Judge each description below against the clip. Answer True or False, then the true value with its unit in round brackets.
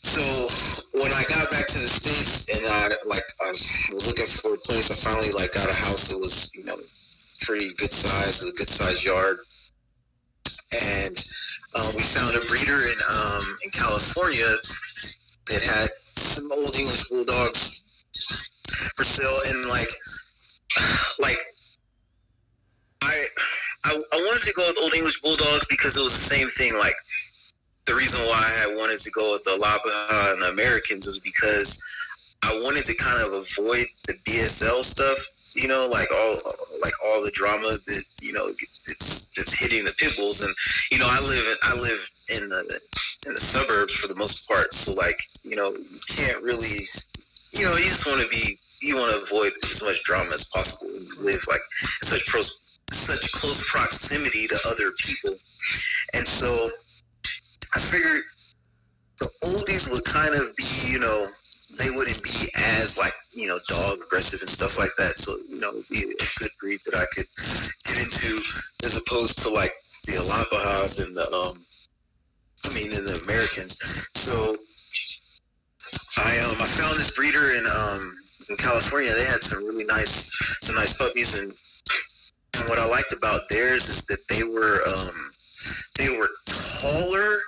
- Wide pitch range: True (6.5 semitones)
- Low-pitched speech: True (115 Hz)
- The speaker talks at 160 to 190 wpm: True (170 wpm)